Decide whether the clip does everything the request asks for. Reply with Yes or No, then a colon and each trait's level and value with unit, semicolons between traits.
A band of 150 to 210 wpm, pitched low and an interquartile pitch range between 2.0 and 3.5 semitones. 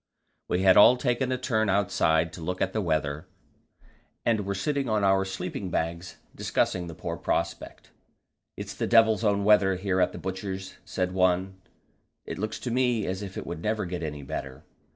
Yes: average, 185 wpm; very low, 95 Hz; average, 3.2 semitones